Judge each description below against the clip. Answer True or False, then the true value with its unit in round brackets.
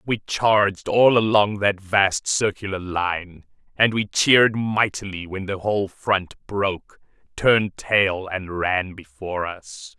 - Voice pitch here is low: True (100 Hz)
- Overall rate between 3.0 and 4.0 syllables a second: True (3.8 syllables/s)